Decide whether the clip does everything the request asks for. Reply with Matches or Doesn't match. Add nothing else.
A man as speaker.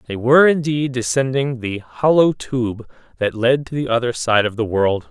Matches